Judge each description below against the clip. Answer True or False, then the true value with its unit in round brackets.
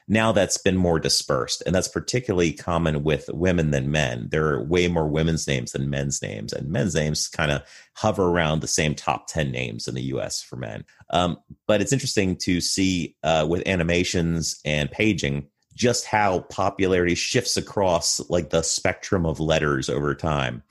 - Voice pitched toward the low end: True (80 Hz)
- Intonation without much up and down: False (3.6 semitones)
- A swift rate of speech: False (180 wpm)